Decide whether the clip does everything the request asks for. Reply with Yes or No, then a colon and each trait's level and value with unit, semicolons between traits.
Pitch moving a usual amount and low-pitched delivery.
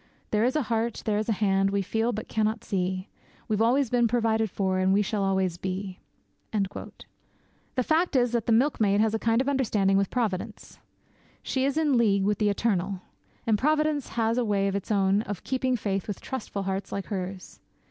No: average, 3.4 semitones; high, 215 Hz